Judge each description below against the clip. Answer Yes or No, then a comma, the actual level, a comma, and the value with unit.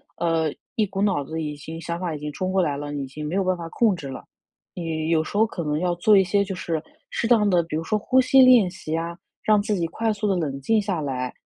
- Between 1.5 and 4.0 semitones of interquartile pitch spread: No, average, 4.5 semitones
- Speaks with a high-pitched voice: No, medium, 175 Hz